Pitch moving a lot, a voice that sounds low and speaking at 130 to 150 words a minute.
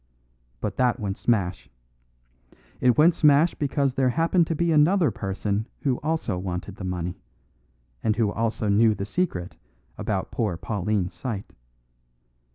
Yes: wide, 6.9 semitones; low, 115 Hz; average, 140 wpm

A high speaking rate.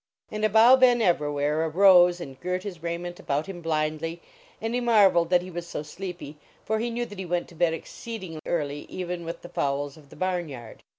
Yes: fast, 215 wpm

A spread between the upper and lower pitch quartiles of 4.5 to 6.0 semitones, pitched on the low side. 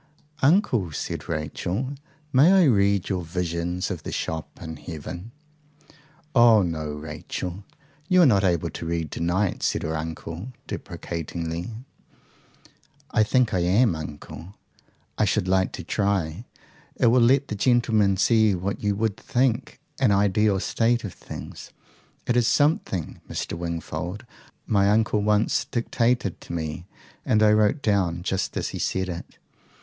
Yes: average, 5.1 semitones; low, 100 Hz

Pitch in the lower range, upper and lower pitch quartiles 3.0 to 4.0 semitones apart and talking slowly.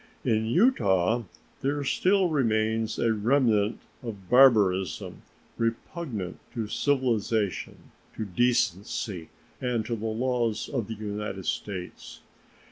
Yes: low, 110 Hz; average, 3.3 semitones; slow, 105 wpm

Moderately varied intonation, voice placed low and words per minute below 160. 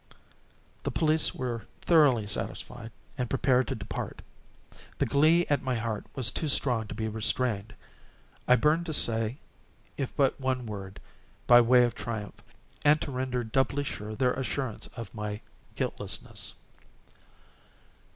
Yes: average, 3.6 semitones; low, 125 Hz; average, 140 wpm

